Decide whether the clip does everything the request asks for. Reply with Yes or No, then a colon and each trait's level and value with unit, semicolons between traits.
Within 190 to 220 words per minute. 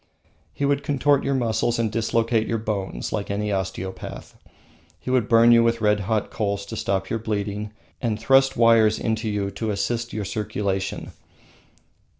No: average, 160 wpm